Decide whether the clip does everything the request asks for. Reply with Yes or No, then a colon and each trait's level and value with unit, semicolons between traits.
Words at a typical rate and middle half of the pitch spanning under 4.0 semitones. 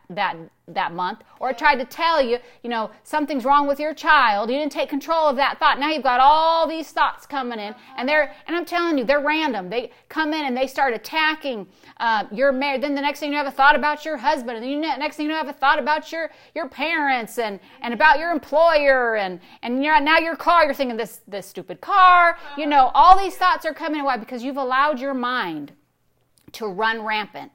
No: fast, 225 wpm; average, 3.5 semitones